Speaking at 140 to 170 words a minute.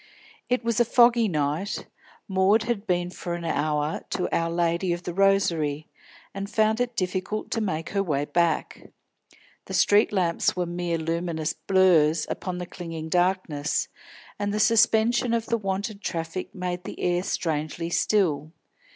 Yes: average, 155 wpm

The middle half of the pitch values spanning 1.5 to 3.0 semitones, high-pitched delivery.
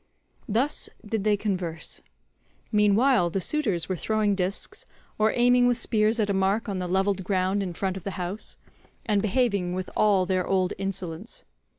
Yes: narrow, 2.6 semitones; high, 195 Hz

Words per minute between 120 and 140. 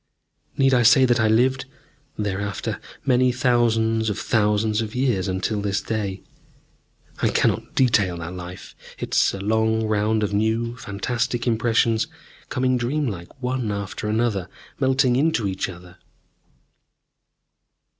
Yes: slow, 135 wpm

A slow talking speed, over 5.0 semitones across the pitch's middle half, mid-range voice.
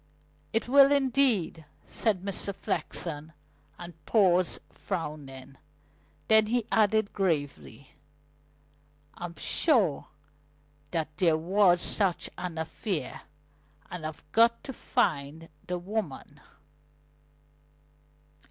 Yes: slow, 90 wpm; wide, 5.5 semitones; medium, 180 Hz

